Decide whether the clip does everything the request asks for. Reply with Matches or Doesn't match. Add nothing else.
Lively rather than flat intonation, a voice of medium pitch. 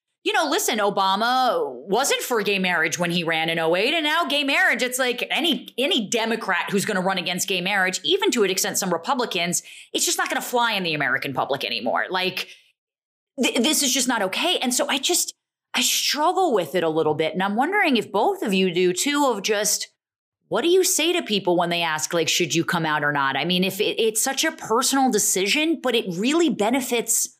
Doesn't match